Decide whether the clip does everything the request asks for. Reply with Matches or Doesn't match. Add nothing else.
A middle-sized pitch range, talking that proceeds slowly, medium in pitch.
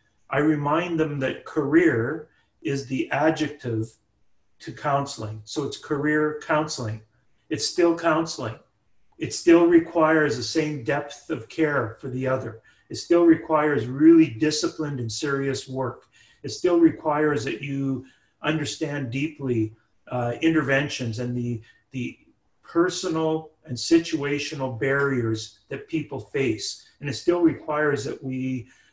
Matches